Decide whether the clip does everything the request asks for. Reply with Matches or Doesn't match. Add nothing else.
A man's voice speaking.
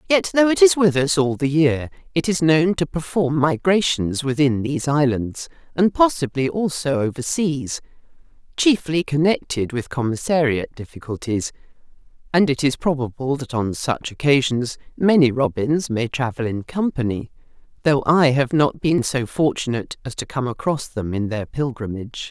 Doesn't match